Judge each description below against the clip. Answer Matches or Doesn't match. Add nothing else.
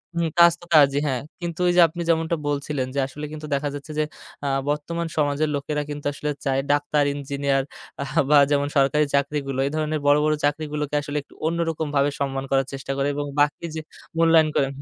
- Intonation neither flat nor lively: Doesn't match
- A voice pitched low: Doesn't match